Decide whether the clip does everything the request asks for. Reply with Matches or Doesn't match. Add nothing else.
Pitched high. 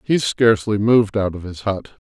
Doesn't match